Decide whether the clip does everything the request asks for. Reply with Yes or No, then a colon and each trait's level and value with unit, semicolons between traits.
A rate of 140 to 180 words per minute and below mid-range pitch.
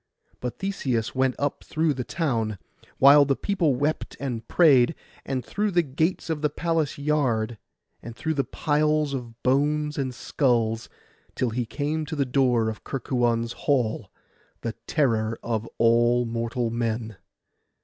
Yes: average, 150 wpm; low, 130 Hz